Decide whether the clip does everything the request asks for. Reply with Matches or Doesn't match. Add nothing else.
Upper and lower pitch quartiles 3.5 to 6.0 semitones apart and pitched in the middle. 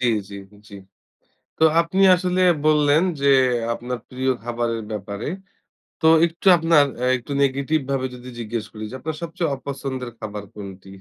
Doesn't match